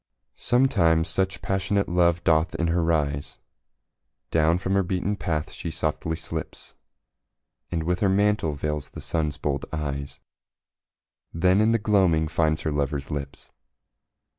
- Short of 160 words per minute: Yes, average, 140 wpm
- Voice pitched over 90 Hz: No, very low, 85 Hz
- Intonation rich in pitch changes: No, average, 3.7 semitones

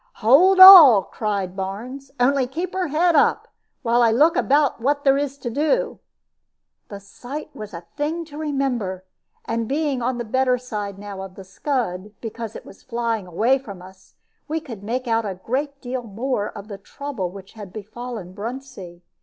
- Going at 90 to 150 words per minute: No, average, 180 wpm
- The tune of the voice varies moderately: No, wide, 5.7 semitones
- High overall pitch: Yes, high, 240 Hz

